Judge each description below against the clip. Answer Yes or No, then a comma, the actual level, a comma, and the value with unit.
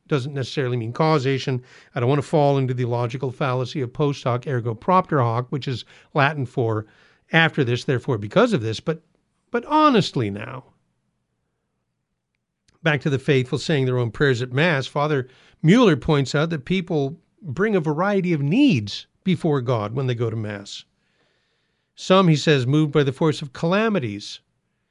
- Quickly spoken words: No, average, 170 wpm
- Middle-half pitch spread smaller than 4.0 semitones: No, average, 4.4 semitones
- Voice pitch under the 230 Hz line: Yes, medium, 140 Hz